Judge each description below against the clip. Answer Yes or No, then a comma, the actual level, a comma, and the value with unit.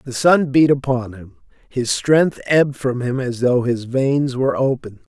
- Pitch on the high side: No, low, 130 Hz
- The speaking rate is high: No, average, 185 wpm